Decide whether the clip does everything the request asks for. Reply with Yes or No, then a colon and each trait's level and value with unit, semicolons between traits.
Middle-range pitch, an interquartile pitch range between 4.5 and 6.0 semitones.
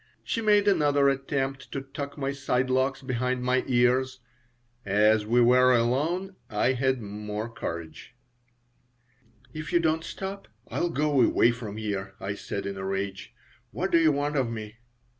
No: low, 130 Hz; average, 4.8 semitones